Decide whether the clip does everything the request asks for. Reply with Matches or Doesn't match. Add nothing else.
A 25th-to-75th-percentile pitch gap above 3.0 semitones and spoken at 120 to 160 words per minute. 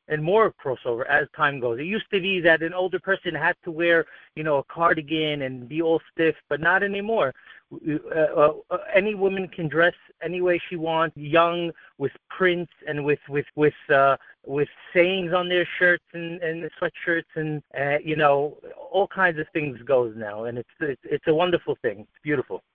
Doesn't match